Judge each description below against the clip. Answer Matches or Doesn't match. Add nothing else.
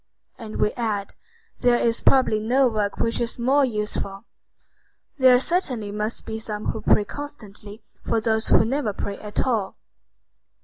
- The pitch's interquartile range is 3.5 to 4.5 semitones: Doesn't match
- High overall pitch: Matches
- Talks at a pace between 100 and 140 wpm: Doesn't match